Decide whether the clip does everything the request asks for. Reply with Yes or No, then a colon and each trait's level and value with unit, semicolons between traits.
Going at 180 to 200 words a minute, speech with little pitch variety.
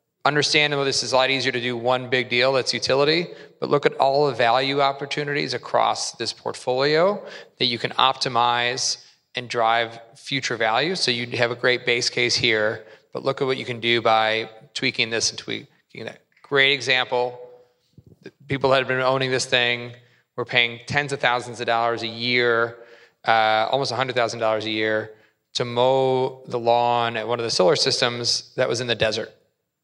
Yes: average, 185 wpm; narrow, 2.1 semitones